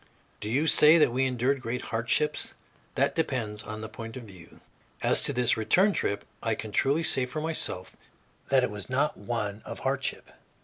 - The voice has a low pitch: Yes, low, 120 Hz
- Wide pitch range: No, average, 4.4 semitones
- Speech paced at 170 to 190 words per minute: Yes, average, 185 wpm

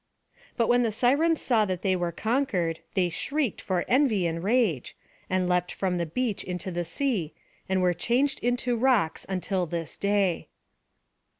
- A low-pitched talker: No, high, 190 Hz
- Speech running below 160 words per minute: No, average, 165 wpm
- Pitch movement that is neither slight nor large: No, wide, 5.7 semitones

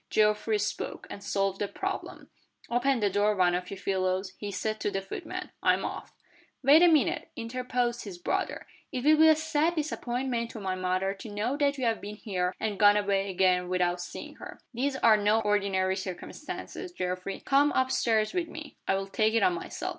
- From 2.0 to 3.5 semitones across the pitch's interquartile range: No, average, 5.1 semitones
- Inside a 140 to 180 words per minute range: No, average, 195 wpm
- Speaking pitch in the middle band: No, high, 210 Hz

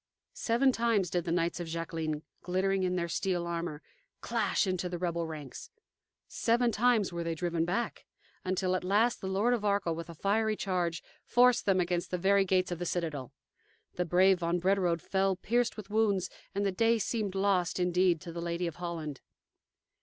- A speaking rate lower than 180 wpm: No, average, 185 wpm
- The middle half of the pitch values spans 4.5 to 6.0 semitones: No, average, 2.8 semitones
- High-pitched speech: No, medium, 180 Hz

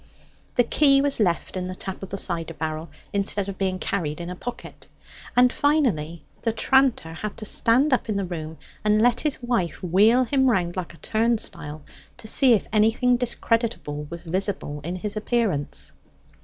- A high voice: Yes, high, 200 Hz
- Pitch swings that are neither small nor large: No, wide, 5.9 semitones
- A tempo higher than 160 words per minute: Yes, average, 180 wpm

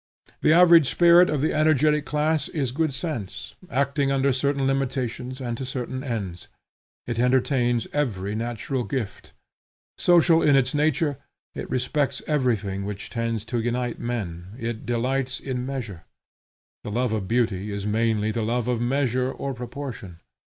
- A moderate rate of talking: Yes, average, 150 wpm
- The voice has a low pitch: Yes, low, 125 Hz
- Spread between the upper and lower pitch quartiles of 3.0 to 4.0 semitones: Yes, average, 3.4 semitones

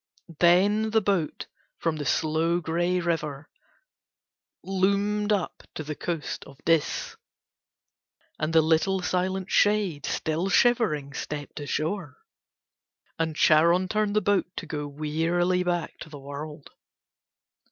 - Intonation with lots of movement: No, average, 3.8 semitones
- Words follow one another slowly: Yes, slow, 120 wpm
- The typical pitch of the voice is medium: Yes, medium, 170 Hz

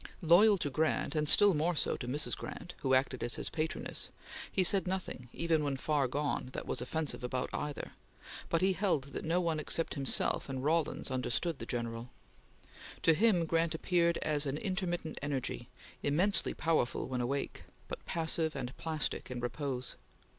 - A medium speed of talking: Yes, average, 170 wpm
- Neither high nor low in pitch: Yes, medium, 155 Hz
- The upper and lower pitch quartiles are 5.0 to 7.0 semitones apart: No, average, 4.0 semitones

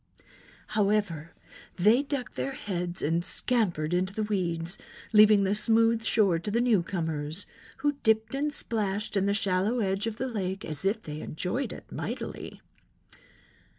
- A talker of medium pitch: No, high, 205 Hz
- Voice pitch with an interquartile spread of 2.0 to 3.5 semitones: No, average, 4.2 semitones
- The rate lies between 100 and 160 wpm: Yes, average, 150 wpm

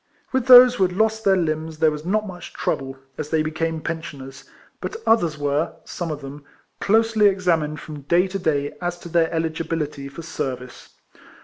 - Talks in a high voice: No, medium, 165 Hz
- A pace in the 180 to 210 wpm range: Yes, average, 185 wpm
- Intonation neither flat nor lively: Yes, average, 3.8 semitones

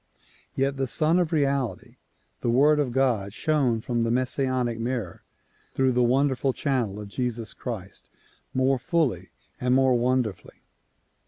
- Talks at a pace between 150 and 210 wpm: No, average, 140 wpm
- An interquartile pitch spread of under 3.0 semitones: Yes, narrow, 2.5 semitones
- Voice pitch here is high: No, low, 130 Hz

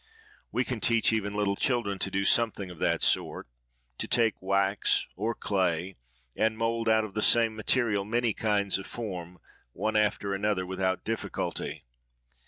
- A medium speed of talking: Yes, average, 155 wpm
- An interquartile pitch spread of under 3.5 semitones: Yes, average, 2.8 semitones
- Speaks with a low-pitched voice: Yes, low, 105 Hz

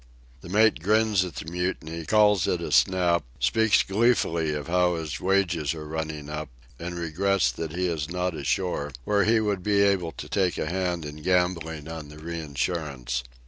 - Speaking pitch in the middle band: No, very low, 85 Hz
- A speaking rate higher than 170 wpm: Yes, average, 180 wpm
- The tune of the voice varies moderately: Yes, average, 3.5 semitones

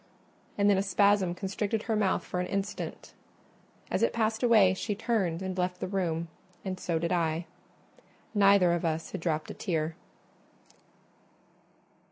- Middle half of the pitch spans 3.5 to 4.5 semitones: No, average, 3.1 semitones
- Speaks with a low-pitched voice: No, high, 190 Hz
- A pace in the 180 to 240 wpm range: No, average, 155 wpm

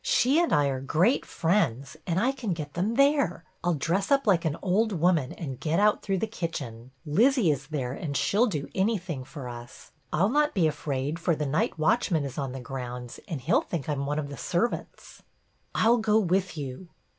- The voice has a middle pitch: Yes, medium, 165 Hz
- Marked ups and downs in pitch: Yes, wide, 6.7 semitones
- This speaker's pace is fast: Yes, fast, 225 wpm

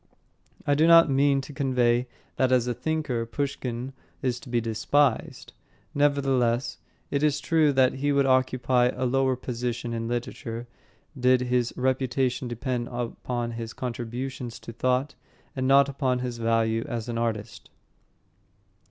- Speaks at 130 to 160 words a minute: Yes, average, 145 wpm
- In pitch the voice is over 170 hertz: No, low, 125 Hz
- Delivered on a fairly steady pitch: Yes, narrow, 2.2 semitones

